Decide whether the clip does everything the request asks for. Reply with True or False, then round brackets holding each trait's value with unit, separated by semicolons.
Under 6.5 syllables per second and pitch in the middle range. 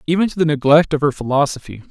False (7.0 syllables/s; 150 Hz)